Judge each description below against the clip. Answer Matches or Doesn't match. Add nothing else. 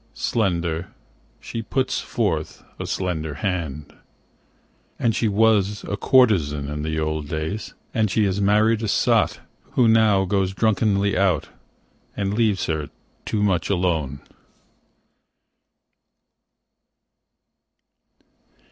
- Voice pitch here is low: Matches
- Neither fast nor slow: Doesn't match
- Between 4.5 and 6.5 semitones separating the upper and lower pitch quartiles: Matches